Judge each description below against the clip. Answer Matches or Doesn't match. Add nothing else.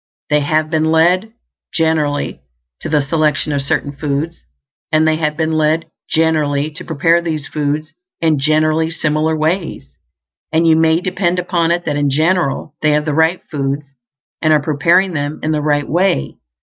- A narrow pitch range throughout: Matches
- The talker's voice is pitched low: Doesn't match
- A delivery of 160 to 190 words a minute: Matches